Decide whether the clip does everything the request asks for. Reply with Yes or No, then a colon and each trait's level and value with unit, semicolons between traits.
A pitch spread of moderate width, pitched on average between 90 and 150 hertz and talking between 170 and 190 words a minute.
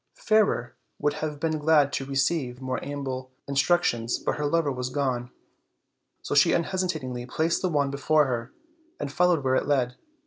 Yes: average, 3.5 semitones; medium, 140 Hz; average, 175 wpm